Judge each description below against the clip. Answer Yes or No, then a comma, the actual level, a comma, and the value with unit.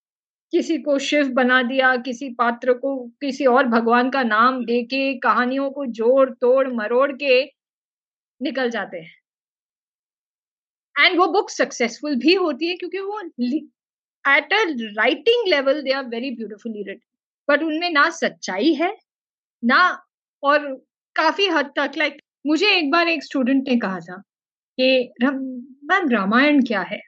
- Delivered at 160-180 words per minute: No, average, 145 wpm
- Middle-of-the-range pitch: No, very high, 270 Hz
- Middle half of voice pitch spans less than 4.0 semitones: Yes, average, 3.5 semitones